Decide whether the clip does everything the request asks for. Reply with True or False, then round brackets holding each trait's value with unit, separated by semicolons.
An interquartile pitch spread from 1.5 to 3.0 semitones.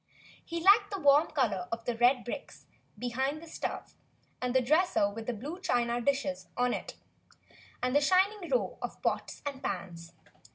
False (5.3 semitones)